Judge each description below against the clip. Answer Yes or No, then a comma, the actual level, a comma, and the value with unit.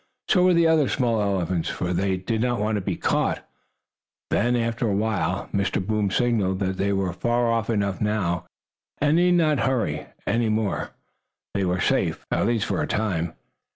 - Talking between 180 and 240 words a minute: Yes, average, 185 wpm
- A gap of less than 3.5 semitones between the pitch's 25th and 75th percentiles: No, average, 3.9 semitones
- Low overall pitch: Yes, low, 105 Hz